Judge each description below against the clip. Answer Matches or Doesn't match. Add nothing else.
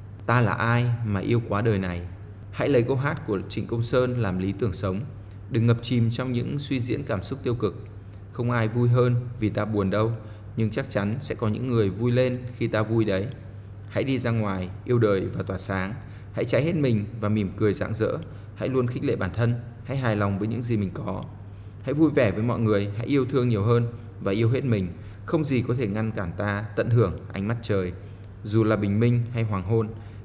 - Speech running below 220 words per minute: Doesn't match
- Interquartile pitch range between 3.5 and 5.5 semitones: Doesn't match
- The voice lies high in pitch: Doesn't match